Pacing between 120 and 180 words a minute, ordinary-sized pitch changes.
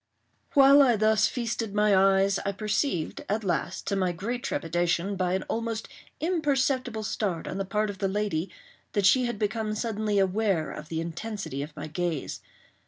Yes: average, 170 wpm; average, 3.4 semitones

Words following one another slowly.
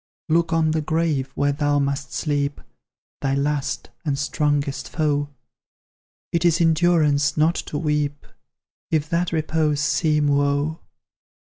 Yes: slow, 125 wpm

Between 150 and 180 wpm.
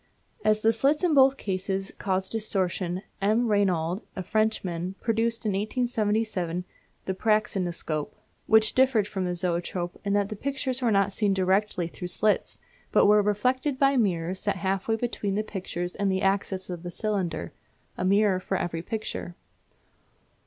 Yes: average, 160 wpm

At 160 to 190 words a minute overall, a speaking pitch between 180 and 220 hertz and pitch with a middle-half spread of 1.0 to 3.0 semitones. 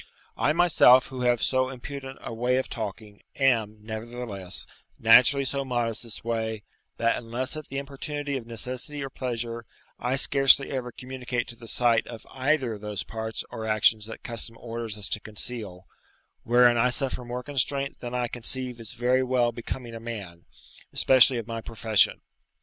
No: average, 170 wpm; low, 120 Hz; narrow, 2.4 semitones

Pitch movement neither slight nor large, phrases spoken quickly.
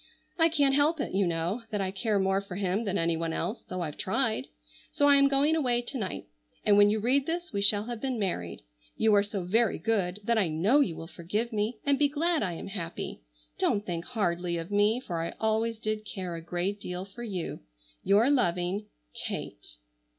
Yes: average, 5.0 semitones; fast, 210 wpm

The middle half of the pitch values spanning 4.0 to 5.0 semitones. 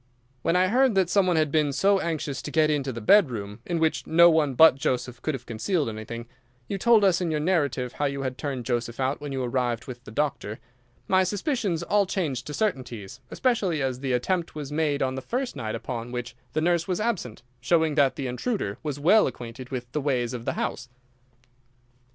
No: wide, 5.6 semitones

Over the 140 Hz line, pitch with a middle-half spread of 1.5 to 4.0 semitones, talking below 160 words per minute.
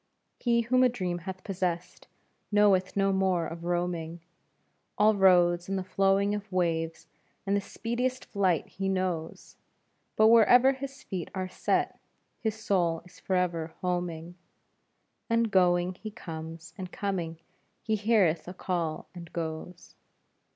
Yes: medium, 185 Hz; average, 3.1 semitones; slow, 135 wpm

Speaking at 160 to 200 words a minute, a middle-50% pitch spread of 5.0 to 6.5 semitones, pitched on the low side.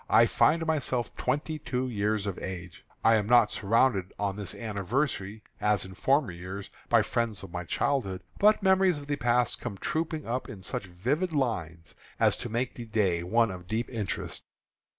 Yes: average, 185 wpm; wide, 5.4 semitones; low, 115 Hz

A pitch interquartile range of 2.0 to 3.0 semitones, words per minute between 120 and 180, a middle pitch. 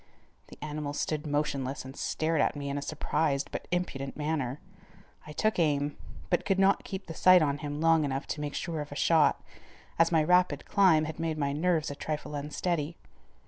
No: narrow, 2.4 semitones; average, 195 wpm; medium, 150 Hz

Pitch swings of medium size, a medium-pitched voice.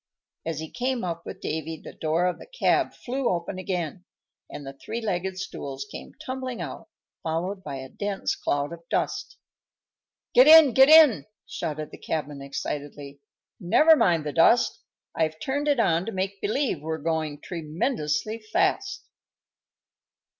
No: wide, 7.1 semitones; medium, 175 Hz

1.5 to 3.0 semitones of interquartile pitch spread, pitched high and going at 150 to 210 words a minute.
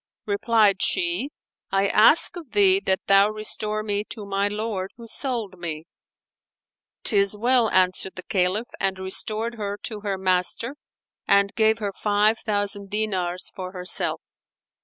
No: narrow, 2.4 semitones; high, 205 Hz; average, 140 wpm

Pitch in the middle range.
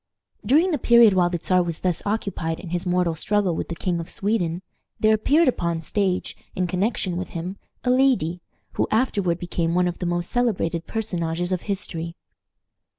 Yes: medium, 180 Hz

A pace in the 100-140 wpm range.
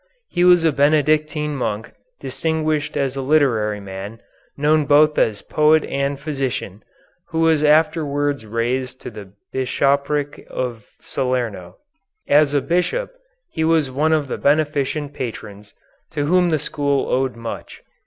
Yes: slow, 135 wpm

